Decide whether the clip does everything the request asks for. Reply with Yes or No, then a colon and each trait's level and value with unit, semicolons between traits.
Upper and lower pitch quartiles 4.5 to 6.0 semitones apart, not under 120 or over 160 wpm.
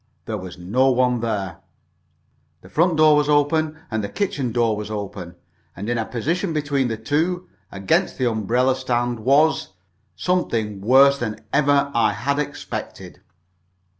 Yes: average, 5.2 semitones; average, 150 wpm